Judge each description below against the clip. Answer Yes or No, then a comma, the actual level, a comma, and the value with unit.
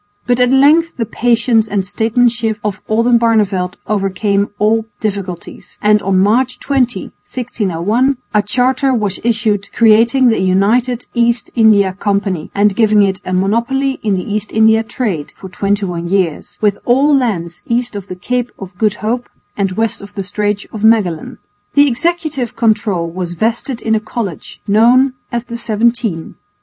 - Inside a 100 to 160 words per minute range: Yes, average, 155 wpm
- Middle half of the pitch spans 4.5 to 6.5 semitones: No, average, 3.3 semitones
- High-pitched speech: Yes, high, 215 Hz